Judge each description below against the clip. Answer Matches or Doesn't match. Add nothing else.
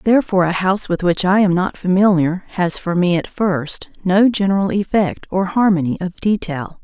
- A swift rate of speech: Doesn't match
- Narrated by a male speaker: Doesn't match